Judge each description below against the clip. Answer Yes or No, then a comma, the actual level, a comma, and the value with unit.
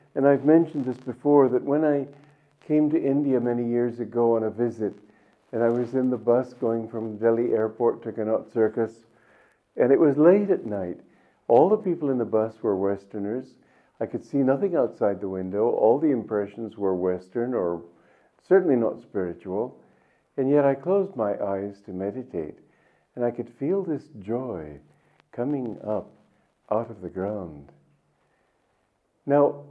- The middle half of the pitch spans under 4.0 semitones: No, average, 4.8 semitones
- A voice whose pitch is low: Yes, low, 120 Hz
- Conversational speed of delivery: Yes, average, 165 wpm